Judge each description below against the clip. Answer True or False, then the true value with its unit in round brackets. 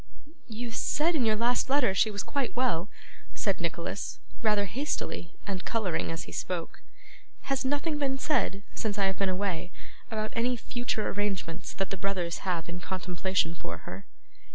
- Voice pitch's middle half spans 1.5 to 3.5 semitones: False (5.0 semitones)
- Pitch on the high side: True (205 Hz)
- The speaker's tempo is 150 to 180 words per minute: True (170 wpm)